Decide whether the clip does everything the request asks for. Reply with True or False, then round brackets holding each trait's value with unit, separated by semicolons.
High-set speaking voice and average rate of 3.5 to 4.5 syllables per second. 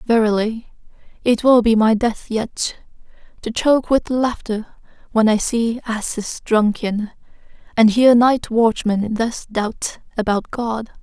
True (225 Hz; 3.8 syllables/s)